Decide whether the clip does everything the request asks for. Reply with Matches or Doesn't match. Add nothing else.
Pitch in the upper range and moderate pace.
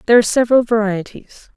Matches